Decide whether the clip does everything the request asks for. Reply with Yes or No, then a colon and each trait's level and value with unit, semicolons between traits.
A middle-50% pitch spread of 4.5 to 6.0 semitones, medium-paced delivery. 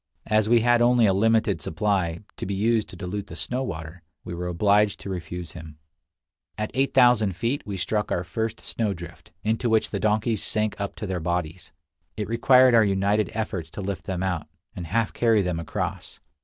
No: average, 4.0 semitones; average, 190 wpm